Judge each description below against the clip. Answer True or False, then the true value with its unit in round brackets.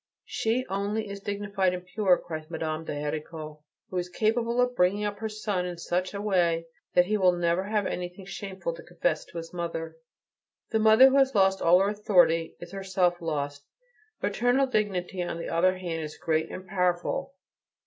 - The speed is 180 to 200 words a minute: True (185 wpm)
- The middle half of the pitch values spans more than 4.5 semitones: False (3.5 semitones)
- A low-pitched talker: False (180 Hz)